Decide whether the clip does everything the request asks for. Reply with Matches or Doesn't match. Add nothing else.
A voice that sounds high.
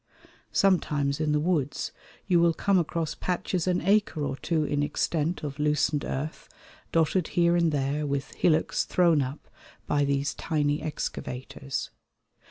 Doesn't match